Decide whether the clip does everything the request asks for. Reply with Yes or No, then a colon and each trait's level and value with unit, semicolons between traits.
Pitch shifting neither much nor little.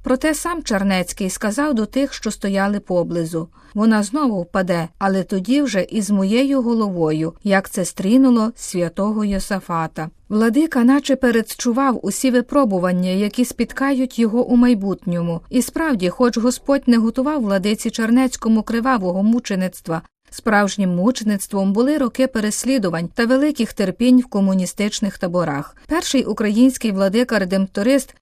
Yes: average, 4.7 semitones